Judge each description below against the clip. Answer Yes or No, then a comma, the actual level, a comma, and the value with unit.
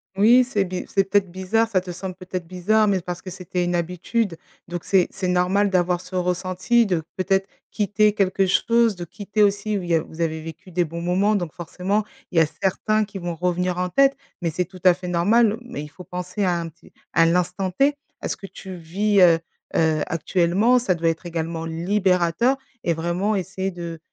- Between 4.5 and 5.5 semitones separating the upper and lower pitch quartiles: No, average, 2.7 semitones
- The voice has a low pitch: No, medium, 185 Hz